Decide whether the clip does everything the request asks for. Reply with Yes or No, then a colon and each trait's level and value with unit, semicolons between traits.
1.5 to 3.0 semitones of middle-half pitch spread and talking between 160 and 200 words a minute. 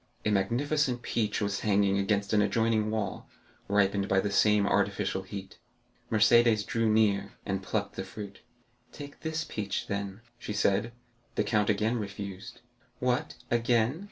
No: narrow, 2.4 semitones; average, 145 wpm